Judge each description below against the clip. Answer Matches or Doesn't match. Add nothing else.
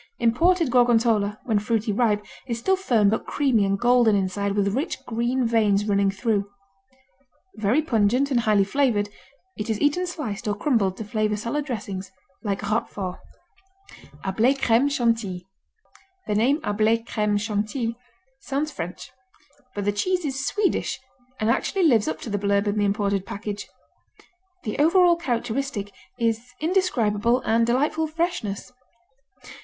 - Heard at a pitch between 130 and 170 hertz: Doesn't match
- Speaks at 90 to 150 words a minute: Matches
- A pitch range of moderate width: Matches